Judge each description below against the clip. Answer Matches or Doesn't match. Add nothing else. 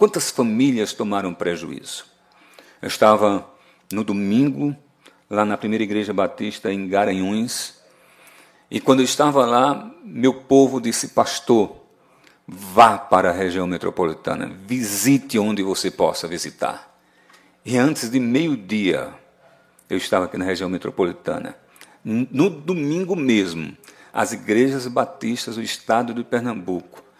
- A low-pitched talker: Matches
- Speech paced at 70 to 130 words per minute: Matches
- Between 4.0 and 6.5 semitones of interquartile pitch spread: Matches